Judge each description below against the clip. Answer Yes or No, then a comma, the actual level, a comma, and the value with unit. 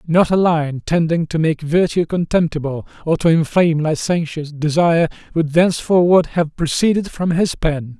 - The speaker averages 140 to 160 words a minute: Yes, average, 150 wpm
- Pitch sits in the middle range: Yes, medium, 165 Hz